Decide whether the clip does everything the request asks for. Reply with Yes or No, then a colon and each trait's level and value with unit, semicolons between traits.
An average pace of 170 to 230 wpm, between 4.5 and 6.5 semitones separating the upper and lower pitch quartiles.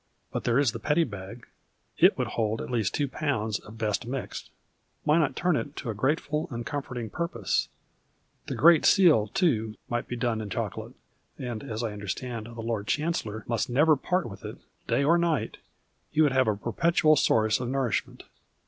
Yes: average, 190 wpm; average, 5.3 semitones